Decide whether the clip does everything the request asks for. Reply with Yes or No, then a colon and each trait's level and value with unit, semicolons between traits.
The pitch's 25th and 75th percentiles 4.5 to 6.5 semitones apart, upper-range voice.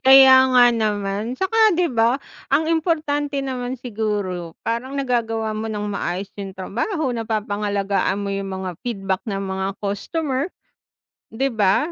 Yes: average, 5.1 semitones; high, 225 Hz